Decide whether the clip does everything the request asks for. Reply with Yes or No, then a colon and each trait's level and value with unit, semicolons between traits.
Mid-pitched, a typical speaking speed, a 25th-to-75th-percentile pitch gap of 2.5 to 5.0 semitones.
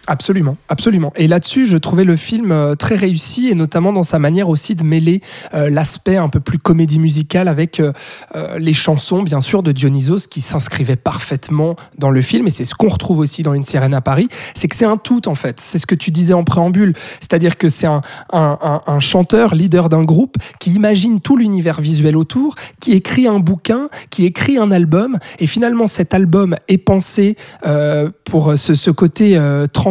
Yes: medium, 170 Hz; average, 205 wpm; average, 4.1 semitones